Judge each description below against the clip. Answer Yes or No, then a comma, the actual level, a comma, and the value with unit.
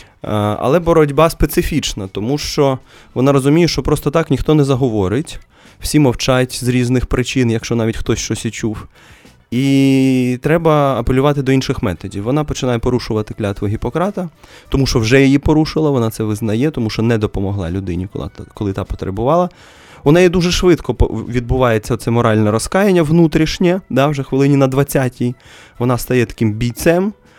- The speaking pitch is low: Yes, low, 130 Hz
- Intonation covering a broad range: No, average, 4.9 semitones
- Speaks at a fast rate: No, average, 150 wpm